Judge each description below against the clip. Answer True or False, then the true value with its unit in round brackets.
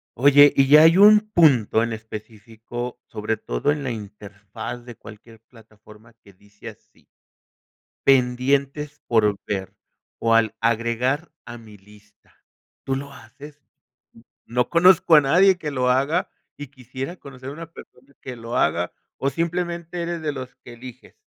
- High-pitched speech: False (125 Hz)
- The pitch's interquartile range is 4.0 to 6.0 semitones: True (4.5 semitones)